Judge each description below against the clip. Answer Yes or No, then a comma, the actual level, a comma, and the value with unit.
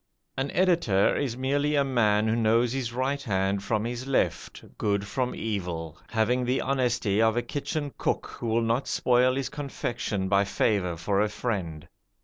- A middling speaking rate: Yes, average, 170 wpm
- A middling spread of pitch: Yes, average, 4.4 semitones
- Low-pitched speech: Yes, low, 115 Hz